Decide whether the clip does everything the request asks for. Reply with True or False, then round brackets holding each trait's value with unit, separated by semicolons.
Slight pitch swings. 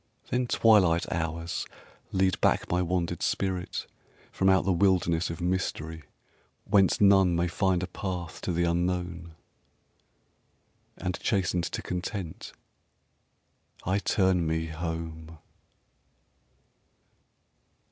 True (2.1 semitones)